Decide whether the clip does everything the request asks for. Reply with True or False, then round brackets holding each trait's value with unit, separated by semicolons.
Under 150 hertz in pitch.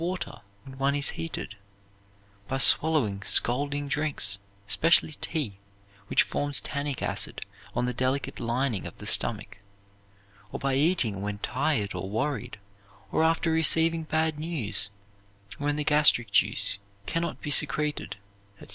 True (140 Hz)